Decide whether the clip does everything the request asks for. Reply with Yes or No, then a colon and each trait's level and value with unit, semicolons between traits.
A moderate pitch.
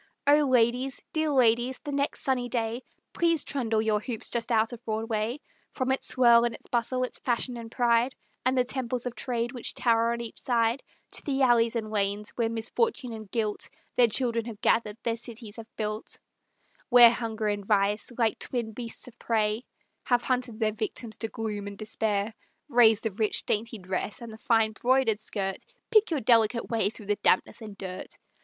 No: high, 230 Hz